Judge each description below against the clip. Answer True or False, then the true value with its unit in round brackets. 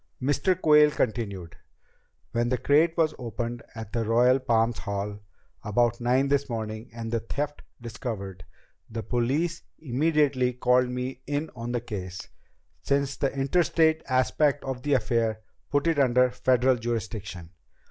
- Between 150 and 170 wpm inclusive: False (140 wpm)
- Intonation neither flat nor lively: True (3.7 semitones)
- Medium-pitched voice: False (125 Hz)